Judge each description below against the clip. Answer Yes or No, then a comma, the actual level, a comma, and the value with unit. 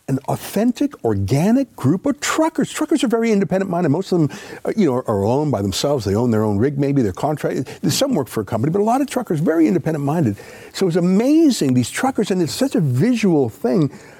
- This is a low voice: No, medium, 170 Hz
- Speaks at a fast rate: Yes, fast, 215 wpm